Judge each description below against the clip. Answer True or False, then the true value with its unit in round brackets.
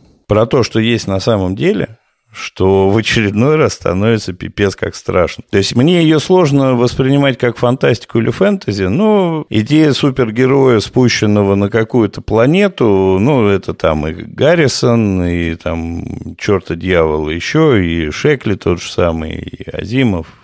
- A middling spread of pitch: False (5.9 semitones)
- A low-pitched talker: True (110 Hz)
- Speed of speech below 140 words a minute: False (145 wpm)